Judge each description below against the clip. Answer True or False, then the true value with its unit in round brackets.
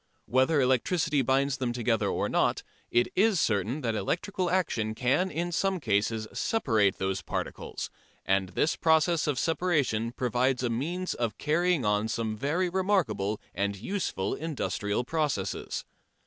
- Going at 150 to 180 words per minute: False (140 wpm)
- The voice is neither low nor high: False (130 Hz)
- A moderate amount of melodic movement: False (7.2 semitones)